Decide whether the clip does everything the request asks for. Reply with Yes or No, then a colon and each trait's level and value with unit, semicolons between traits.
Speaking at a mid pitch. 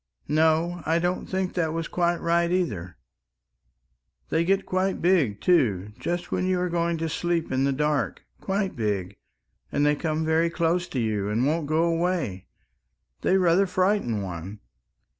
Yes: medium, 165 Hz